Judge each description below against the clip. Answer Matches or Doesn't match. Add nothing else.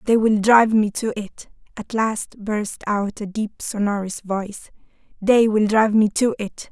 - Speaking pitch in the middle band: Doesn't match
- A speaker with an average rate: Matches